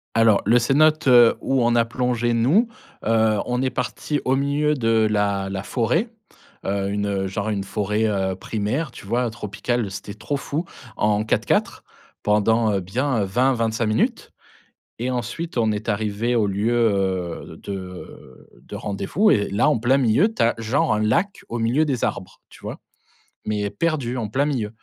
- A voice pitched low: Yes, low, 115 Hz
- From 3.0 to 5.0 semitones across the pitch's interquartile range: Yes, average, 3.7 semitones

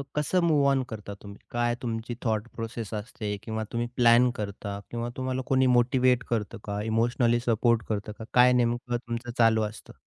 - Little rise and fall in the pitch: Yes, narrow, 1.9 semitones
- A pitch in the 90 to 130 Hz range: Yes, low, 120 Hz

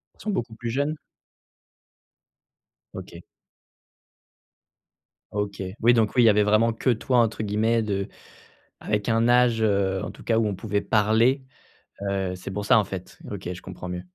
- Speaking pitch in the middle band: No, low, 110 Hz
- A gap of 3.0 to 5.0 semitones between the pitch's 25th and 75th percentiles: No, narrow, 2.6 semitones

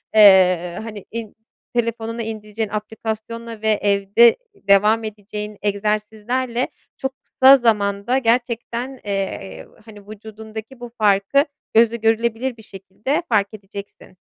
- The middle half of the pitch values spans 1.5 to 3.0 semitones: Yes, narrow, 2.4 semitones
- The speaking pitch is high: Yes, high, 220 Hz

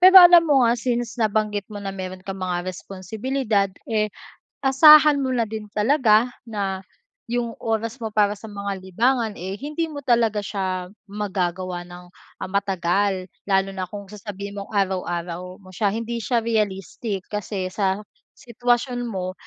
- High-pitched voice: Yes, high, 205 Hz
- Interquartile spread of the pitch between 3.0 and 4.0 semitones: Yes, average, 3.6 semitones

